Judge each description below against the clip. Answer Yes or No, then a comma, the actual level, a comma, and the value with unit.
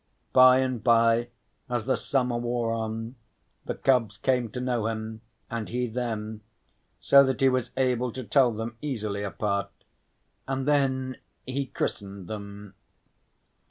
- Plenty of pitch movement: No, average, 2.8 semitones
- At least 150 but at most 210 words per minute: No, average, 140 wpm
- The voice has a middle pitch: No, low, 120 Hz